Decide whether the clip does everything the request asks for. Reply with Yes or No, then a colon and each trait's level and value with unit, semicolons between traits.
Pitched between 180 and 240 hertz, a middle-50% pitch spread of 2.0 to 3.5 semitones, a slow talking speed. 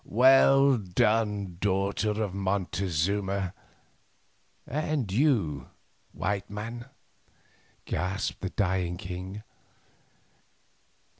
No: low, 100 Hz; average, 2.9 semitones; slow, 70 wpm